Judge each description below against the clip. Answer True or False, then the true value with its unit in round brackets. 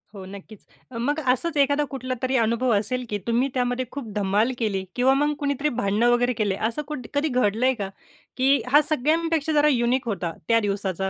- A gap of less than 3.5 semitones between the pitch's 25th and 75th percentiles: False (4.7 semitones)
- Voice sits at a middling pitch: False (250 Hz)